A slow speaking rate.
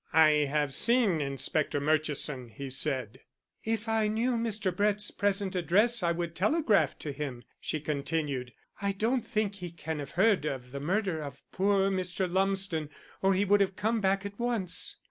No: average, 170 wpm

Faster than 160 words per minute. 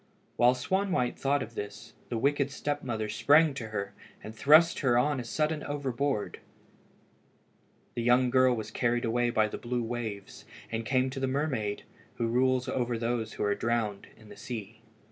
Yes: average, 180 wpm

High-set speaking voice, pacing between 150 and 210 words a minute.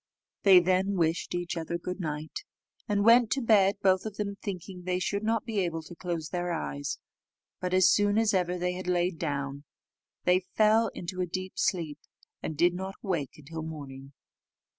No: medium, 180 Hz; average, 185 wpm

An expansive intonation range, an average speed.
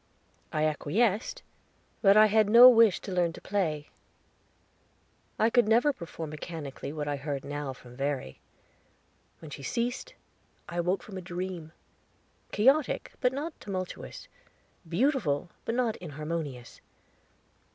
No: wide, 7.1 semitones; slow, 125 wpm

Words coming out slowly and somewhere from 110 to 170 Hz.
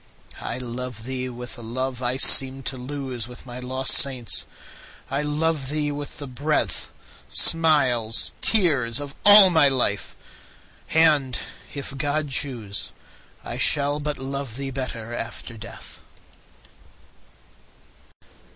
Yes: slow, 115 wpm; low, 135 Hz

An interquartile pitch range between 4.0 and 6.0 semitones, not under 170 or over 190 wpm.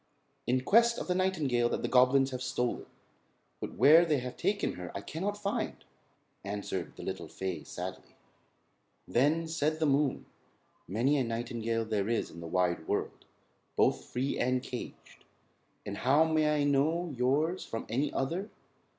No: average, 5.3 semitones; average, 160 wpm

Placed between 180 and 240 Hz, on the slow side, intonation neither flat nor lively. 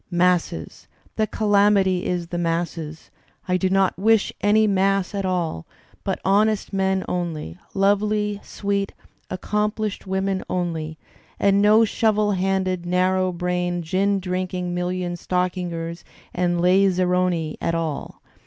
No: medium, 185 Hz; slow, 125 wpm; narrow, 2.1 semitones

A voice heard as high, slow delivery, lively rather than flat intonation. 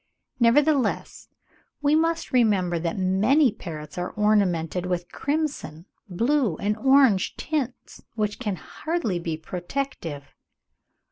Yes: high, 210 Hz; slow, 110 wpm; wide, 7.7 semitones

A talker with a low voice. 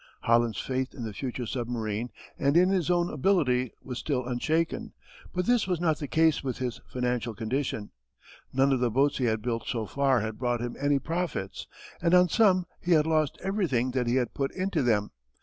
Yes: low, 130 Hz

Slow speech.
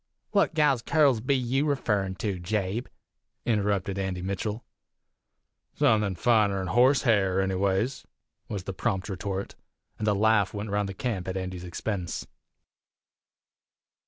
Yes: slow, 130 wpm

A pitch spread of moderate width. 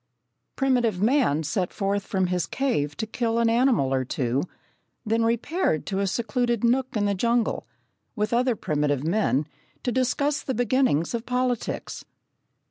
No: wide, 5.7 semitones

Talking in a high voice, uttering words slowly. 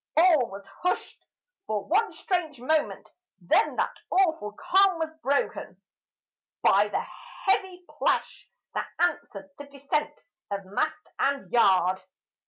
Yes: very high, 285 Hz; slow, 120 wpm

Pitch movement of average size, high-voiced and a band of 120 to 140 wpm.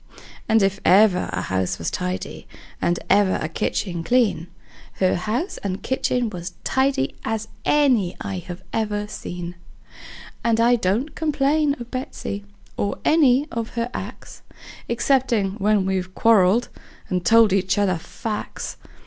Yes: average, 4.7 semitones; high, 210 Hz; slow, 135 wpm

